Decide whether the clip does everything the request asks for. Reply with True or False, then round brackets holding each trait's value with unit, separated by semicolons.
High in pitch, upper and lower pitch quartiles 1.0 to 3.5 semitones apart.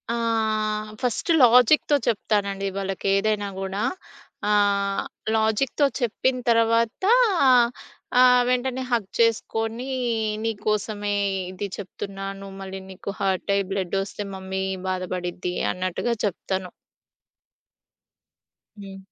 True (205 Hz; 2.9 semitones)